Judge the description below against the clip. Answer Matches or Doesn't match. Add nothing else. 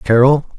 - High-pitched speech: Doesn't match